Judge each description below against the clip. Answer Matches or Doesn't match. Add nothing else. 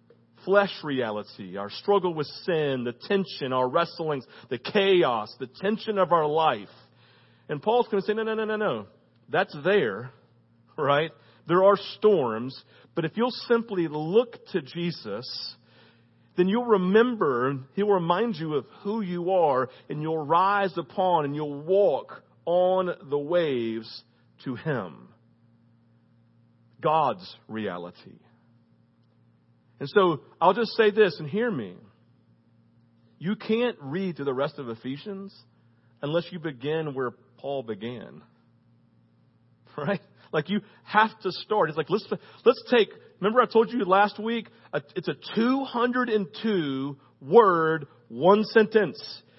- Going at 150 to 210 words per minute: Doesn't match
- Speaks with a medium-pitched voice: Matches